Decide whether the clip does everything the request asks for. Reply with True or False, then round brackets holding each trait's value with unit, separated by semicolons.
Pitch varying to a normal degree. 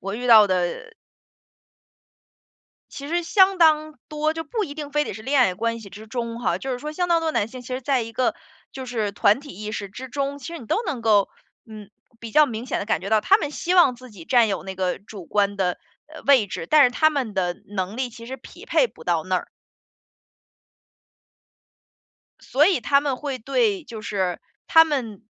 False (6.2 semitones)